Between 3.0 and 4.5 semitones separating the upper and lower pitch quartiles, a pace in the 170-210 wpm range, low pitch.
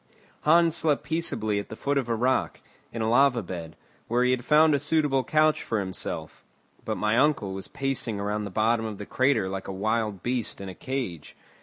No: average, 5.2 semitones; fast, 205 wpm; low, 115 Hz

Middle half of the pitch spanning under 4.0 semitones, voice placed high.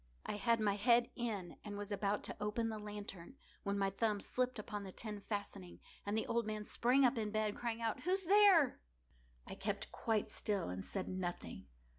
Yes: narrow, 2.6 semitones; high, 210 Hz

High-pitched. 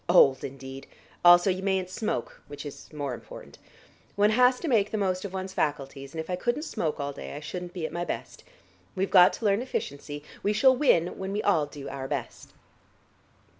No: medium, 180 Hz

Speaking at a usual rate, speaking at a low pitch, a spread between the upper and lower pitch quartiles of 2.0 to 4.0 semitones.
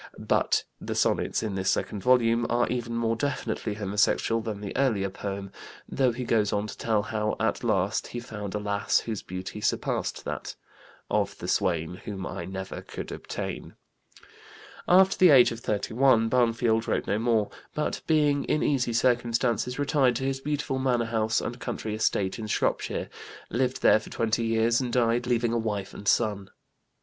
Yes: average, 175 wpm; low, 115 Hz; average, 3.0 semitones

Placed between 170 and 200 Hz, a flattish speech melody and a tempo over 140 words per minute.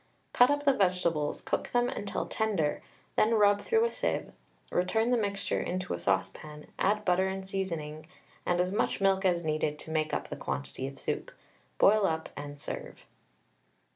No: medium, 185 Hz; average, 5.2 semitones; average, 170 wpm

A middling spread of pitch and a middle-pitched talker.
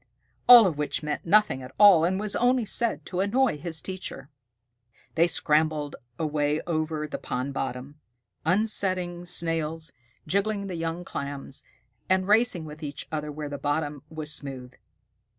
Yes: average, 4.2 semitones; medium, 160 Hz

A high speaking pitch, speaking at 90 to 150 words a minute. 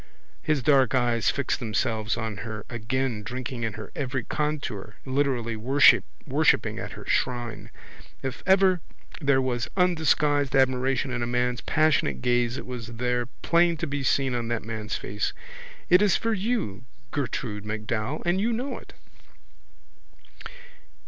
No: low, 125 Hz; average, 140 wpm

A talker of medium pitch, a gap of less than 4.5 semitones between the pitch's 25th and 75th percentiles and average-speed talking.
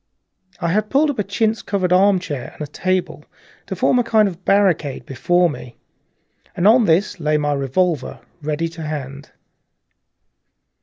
No: medium, 175 Hz; average, 5.2 semitones; average, 150 wpm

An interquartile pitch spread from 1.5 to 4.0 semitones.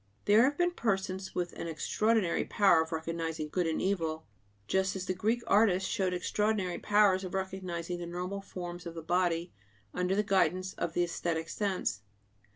Yes: narrow, 2.6 semitones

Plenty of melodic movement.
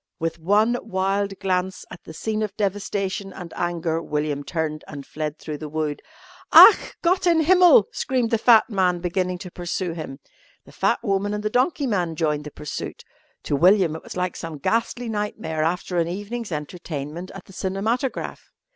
No: average, 4.6 semitones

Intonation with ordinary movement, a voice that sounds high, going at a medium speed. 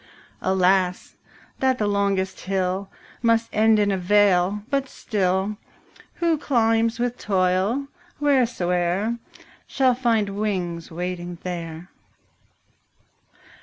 No: average, 4.0 semitones; high, 200 Hz; slow, 100 wpm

